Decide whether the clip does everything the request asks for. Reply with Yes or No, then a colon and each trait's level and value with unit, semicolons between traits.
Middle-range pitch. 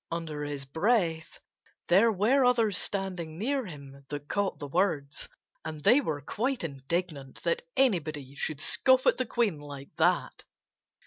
Yes: medium, 165 Hz